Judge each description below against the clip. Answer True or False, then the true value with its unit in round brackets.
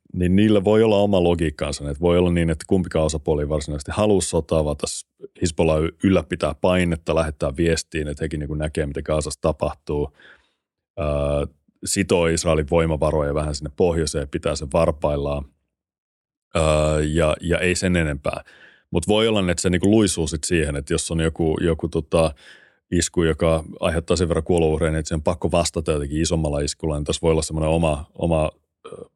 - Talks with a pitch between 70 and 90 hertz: True (80 Hz)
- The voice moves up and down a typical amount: False (2.2 semitones)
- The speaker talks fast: True (175 wpm)